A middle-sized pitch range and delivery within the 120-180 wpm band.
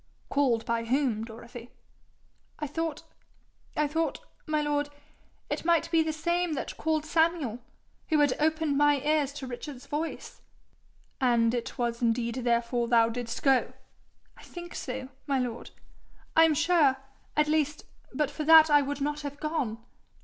Yes: average, 4.2 semitones; average, 155 wpm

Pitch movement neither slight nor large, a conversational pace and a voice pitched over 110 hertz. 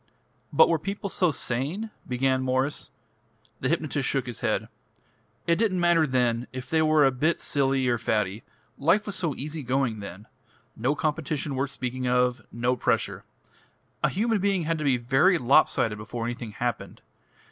Yes: average, 4.6 semitones; average, 170 wpm; low, 135 Hz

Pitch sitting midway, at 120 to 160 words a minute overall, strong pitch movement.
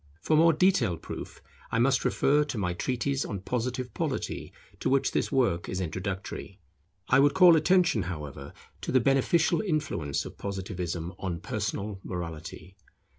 No: low, 115 Hz; average, 150 wpm; wide, 7.7 semitones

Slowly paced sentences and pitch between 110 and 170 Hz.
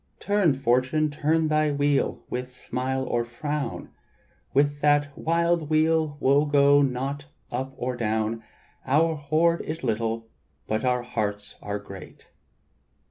Yes: slow, 130 wpm; medium, 140 Hz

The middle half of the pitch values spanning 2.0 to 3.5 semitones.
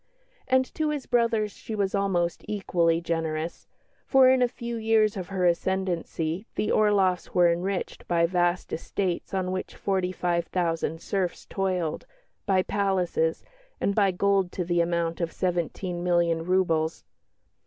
Yes: average, 2.7 semitones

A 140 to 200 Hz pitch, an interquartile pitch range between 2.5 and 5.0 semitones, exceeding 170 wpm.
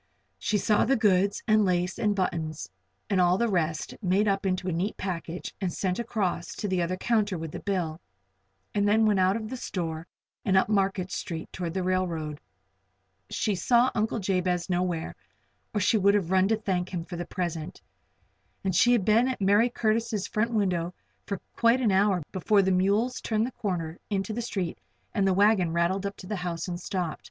Yes: high, 190 Hz; average, 2.9 semitones; average, 200 wpm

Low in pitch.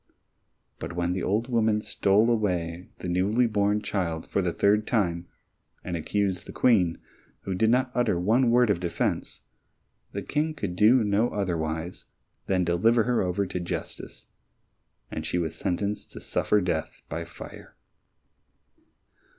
Yes: low, 100 Hz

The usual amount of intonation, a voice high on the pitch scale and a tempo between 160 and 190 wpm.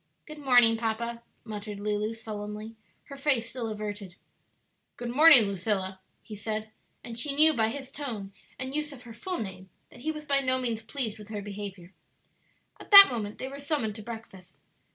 Yes: average, 4.2 semitones; high, 225 Hz; average, 180 wpm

